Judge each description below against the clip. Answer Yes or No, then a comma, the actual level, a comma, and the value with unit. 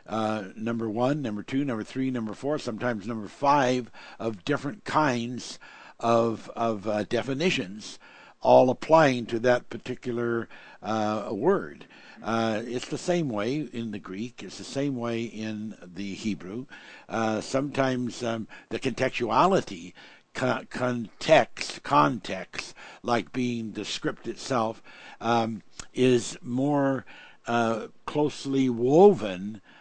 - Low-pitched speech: Yes, low, 120 Hz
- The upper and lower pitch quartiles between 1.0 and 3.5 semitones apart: Yes, average, 3.1 semitones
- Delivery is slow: Yes, slow, 120 wpm